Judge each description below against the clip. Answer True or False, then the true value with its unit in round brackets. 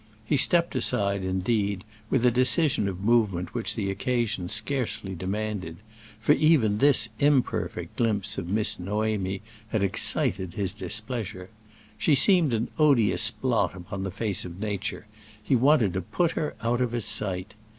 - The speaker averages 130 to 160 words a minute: True (150 wpm)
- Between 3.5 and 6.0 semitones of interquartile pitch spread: True (4.2 semitones)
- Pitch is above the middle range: False (110 Hz)